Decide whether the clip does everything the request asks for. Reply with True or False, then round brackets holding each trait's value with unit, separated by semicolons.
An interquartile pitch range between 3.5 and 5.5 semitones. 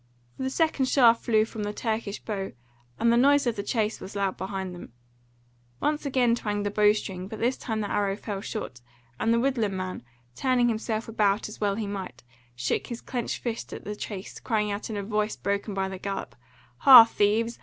False (2.7 semitones)